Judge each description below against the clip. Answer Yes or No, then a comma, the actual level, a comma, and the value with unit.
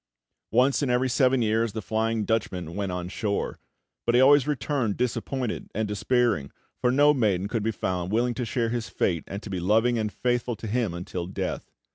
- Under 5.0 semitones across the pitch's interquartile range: Yes, average, 3.6 semitones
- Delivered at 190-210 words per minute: Yes, average, 195 wpm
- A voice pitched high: No, low, 115 Hz